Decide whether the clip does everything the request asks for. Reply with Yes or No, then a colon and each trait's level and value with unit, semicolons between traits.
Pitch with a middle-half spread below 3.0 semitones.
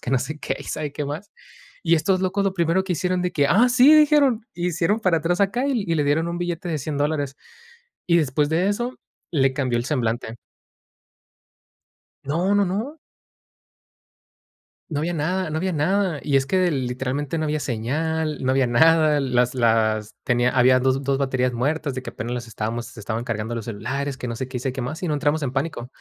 No: wide, 5.4 semitones